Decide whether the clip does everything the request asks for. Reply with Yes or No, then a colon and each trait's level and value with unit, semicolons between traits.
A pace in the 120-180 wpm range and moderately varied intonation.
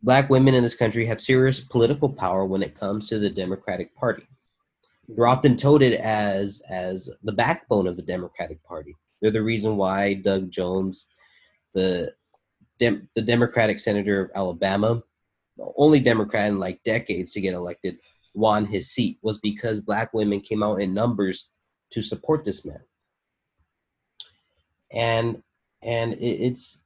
Yes: average, 150 wpm; average, 3.3 semitones